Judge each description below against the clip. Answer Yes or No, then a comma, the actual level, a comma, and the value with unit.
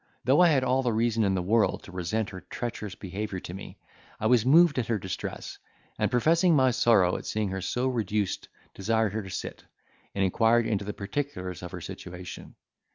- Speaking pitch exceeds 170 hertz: No, low, 110 Hz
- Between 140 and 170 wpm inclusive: No, average, 200 wpm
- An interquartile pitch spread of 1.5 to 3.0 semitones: No, average, 4.3 semitones